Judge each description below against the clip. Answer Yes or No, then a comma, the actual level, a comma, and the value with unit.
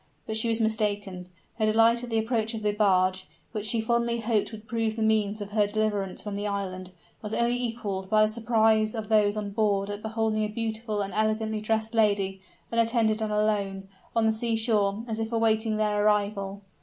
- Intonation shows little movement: Yes, narrow, 1.4 semitones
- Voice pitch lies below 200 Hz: No, high, 215 Hz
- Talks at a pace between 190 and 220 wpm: Yes, average, 195 wpm